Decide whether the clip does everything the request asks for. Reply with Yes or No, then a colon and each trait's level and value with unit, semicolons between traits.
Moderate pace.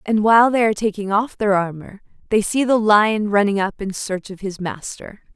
No: fast, 215 wpm